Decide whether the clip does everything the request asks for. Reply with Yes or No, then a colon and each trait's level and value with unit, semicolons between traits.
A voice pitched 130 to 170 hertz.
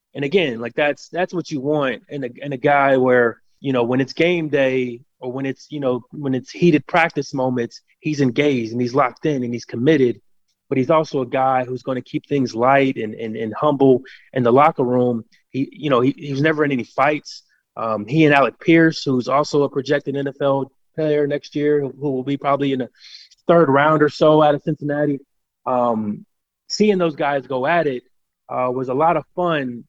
Yes: medium, 140 Hz